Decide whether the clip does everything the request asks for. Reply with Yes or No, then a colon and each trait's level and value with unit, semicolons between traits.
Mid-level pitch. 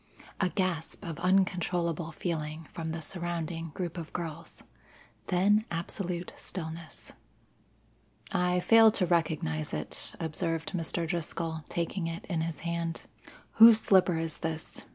Yes: medium, 170 Hz